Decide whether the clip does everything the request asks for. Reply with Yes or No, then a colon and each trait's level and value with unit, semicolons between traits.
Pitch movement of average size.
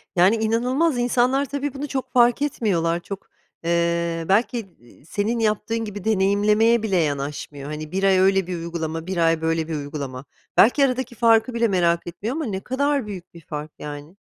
No: wide, 6.1 semitones